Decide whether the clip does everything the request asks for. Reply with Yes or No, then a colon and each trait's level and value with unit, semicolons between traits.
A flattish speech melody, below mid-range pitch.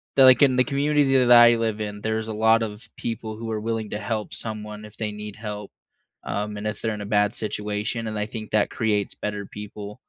Yes: narrow, 1.5 semitones; low, 110 Hz